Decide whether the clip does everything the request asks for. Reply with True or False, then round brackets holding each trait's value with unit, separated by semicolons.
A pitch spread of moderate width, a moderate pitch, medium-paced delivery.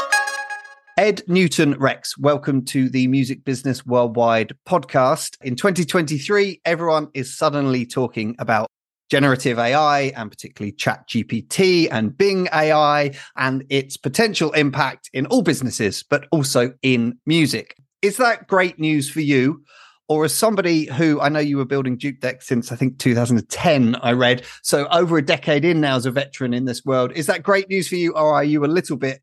True (4.3 semitones; 145 Hz; 170 wpm)